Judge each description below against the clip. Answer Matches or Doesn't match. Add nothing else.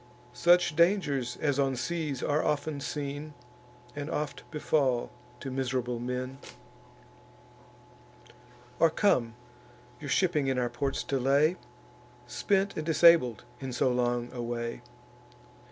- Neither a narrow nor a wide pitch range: Matches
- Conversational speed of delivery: Doesn't match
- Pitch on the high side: Doesn't match